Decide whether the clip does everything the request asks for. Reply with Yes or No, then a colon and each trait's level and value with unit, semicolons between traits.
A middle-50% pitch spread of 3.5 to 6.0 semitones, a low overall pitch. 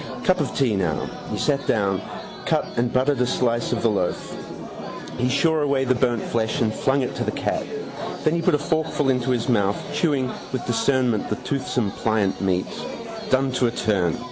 Yes: average, 4.1 semitones; low, 125 Hz